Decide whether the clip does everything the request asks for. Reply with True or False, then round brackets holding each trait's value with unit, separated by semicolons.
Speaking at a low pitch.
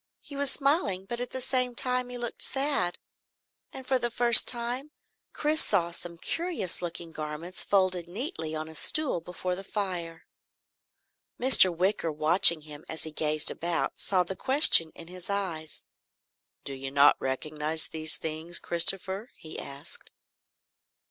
False (180 Hz)